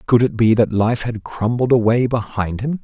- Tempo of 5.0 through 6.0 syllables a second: No, 4.8 syllables/s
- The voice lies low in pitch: Yes, low, 115 Hz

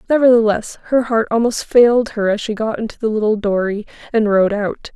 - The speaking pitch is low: No, high, 220 Hz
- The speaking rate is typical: Yes, average, 195 wpm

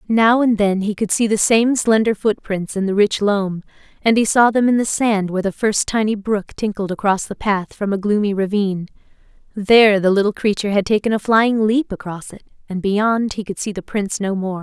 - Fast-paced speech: Yes, fast, 225 wpm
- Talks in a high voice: Yes, high, 205 Hz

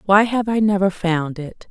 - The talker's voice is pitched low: No, high, 195 Hz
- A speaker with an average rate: No, fast, 210 wpm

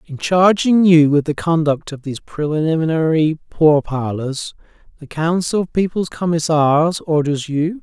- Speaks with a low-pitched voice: No, medium, 160 Hz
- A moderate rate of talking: No, slow, 130 wpm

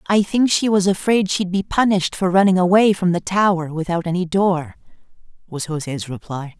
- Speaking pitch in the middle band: Yes, medium, 180 Hz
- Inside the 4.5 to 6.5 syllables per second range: Yes, 5.2 syllables/s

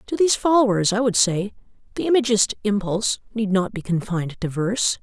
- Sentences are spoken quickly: No, average, 180 wpm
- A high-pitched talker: Yes, high, 210 Hz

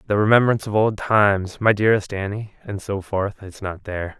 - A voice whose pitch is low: Yes, low, 100 Hz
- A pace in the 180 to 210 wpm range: No, average, 170 wpm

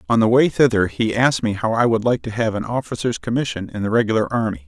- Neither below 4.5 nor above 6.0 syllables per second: No, 6.5 syllables/s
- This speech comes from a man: Yes, male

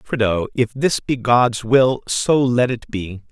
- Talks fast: No, average, 180 wpm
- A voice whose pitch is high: No, low, 120 Hz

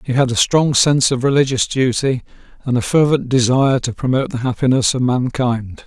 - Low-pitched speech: Yes, low, 130 Hz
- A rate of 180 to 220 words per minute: Yes, average, 185 wpm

